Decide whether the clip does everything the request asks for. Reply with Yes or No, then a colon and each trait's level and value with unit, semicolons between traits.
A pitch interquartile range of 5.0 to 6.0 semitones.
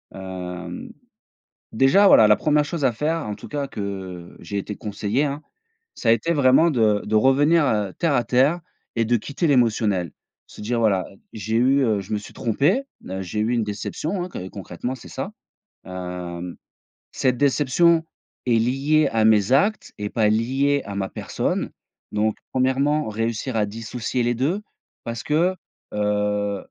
Yes: average, 5.3 semitones